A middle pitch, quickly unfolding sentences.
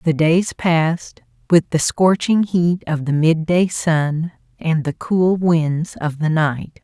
No: medium, 165 Hz; average, 160 wpm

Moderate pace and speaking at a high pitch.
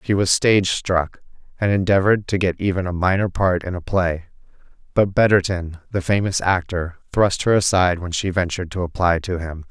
No: average, 185 wpm; very low, 90 Hz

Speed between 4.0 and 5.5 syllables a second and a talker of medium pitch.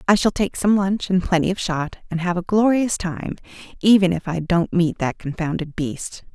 Yes: 4.9 syllables/s; medium, 180 Hz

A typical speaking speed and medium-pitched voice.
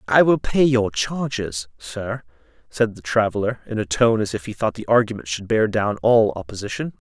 No: average, 195 wpm; low, 110 Hz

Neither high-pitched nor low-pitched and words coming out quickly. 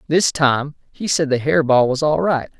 Yes: medium, 145 Hz; fast, 230 wpm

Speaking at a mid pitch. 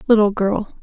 No: high, 205 Hz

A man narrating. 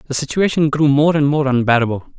Yes: male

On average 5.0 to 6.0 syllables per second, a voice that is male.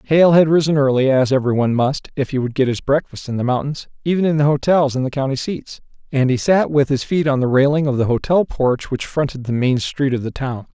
Yes: 5.8 syllables/s; male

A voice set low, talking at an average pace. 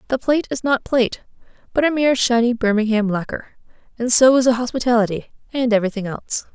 No: high, 240 Hz; average, 175 wpm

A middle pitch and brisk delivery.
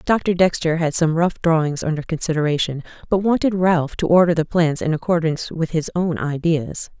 No: medium, 165 Hz; average, 180 wpm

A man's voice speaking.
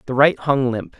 Yes: male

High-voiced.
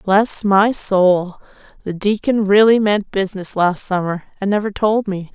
Yes: high, 200 Hz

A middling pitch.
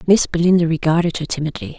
Yes: medium, 165 Hz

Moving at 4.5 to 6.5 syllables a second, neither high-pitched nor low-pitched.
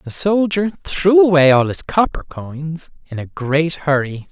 No: 4.0 syllables/s; medium, 160 Hz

